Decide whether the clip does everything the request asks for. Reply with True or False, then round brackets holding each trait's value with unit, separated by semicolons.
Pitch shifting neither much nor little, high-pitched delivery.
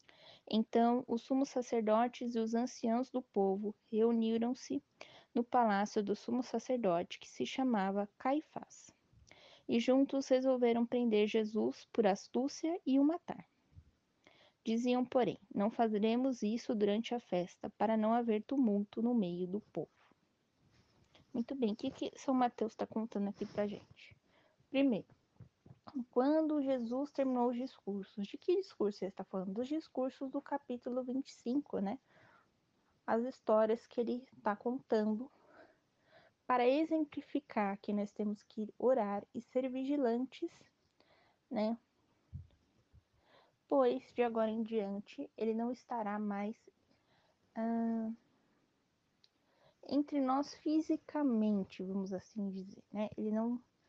True (3.5 semitones; 240 Hz)